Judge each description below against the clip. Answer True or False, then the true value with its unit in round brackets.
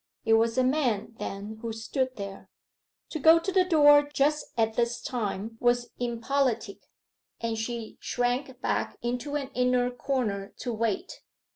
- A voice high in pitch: True (245 Hz)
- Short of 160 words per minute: True (150 wpm)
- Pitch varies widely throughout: False (3.5 semitones)